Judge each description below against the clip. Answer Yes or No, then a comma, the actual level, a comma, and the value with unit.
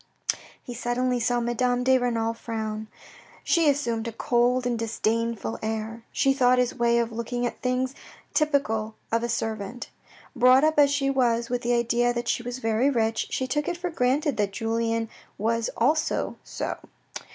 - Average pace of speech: Yes, average, 170 wpm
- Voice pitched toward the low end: No, high, 240 Hz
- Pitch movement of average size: No, narrow, 2.0 semitones